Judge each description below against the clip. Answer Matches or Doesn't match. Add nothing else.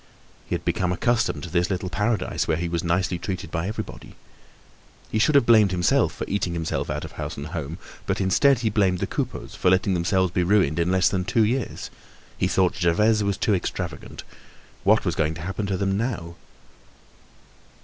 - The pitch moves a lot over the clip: Doesn't match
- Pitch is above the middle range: Doesn't match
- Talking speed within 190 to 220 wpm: Matches